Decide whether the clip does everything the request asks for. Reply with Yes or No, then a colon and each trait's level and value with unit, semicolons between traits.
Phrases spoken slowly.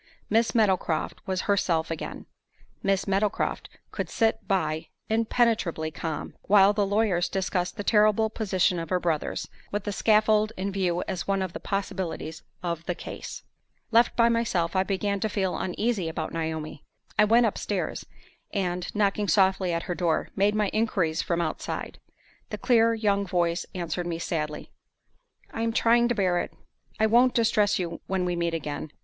No: average, 165 wpm